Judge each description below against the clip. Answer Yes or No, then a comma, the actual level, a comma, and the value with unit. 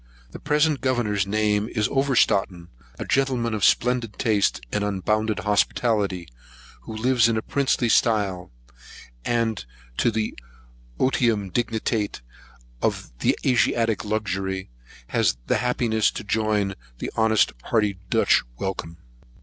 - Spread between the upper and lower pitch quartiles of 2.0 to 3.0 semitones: Yes, average, 2.7 semitones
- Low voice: Yes, low, 110 Hz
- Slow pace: Yes, slow, 115 wpm